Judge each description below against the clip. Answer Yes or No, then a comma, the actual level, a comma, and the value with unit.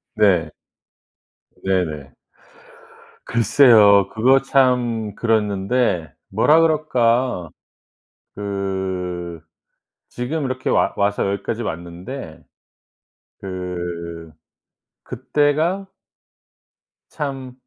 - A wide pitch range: Yes, wide, 6.2 semitones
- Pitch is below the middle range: Yes, low, 105 Hz